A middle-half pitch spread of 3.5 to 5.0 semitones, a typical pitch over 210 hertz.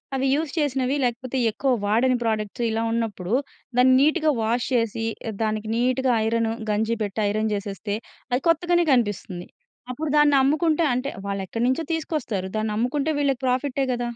Yes: average, 4.0 semitones; high, 245 Hz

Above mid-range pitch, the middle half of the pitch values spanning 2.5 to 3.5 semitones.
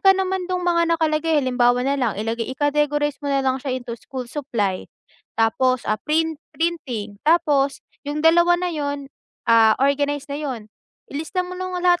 No: very high, 290 Hz; average, 4.6 semitones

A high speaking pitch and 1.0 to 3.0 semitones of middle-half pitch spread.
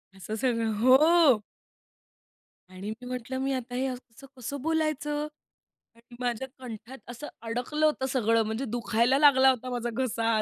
Yes: very high, 250 Hz; average, 2.7 semitones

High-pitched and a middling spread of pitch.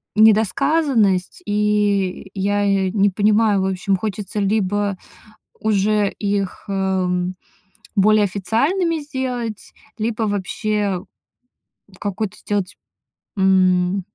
No: high, 205 Hz; narrow, 2.0 semitones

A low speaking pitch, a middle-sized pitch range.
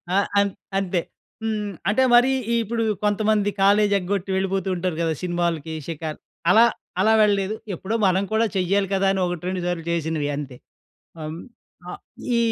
No: high, 190 Hz; average, 3.2 semitones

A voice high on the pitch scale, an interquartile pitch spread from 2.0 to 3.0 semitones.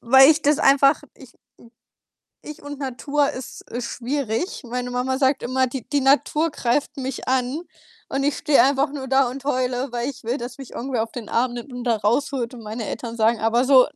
Yes: very high, 260 Hz; narrow, 2.5 semitones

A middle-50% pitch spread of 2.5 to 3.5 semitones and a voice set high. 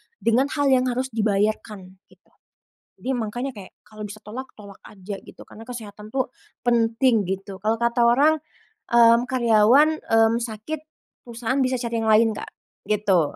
Yes: average, 3.1 semitones; high, 230 Hz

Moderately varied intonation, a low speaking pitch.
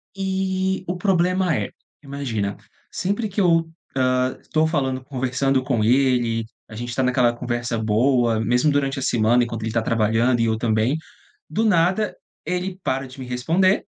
No: wide, 6.2 semitones; low, 130 Hz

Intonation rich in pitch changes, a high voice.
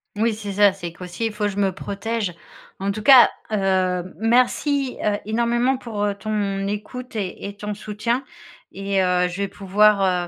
No: narrow, 2.6 semitones; high, 205 Hz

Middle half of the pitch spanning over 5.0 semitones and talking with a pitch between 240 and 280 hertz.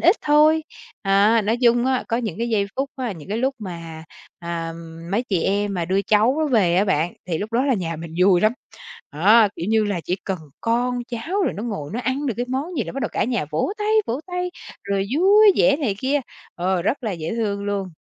No: wide, 5.6 semitones; high, 220 Hz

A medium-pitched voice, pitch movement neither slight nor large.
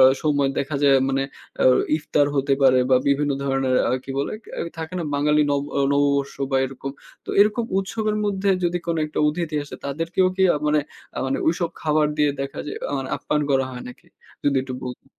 Yes: medium, 145 Hz; average, 3.1 semitones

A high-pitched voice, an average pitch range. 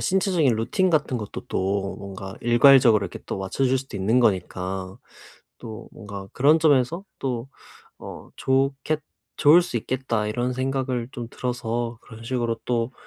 No: low, 120 Hz; average, 4.0 semitones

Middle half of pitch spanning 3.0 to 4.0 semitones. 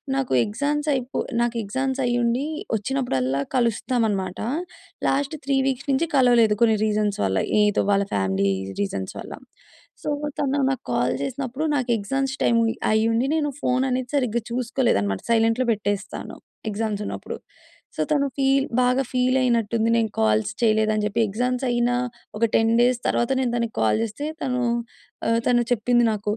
Yes: average, 3.6 semitones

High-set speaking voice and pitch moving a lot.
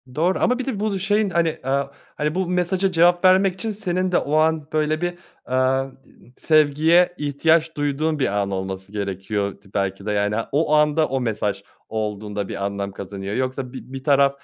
No: medium, 145 Hz; wide, 8.6 semitones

